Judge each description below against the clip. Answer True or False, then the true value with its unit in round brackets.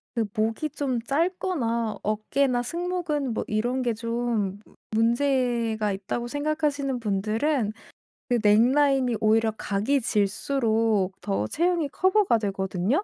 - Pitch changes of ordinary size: True (4.7 semitones)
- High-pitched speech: True (235 Hz)